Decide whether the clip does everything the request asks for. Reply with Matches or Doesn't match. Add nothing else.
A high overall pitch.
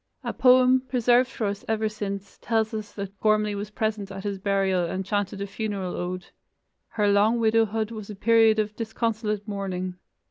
Matches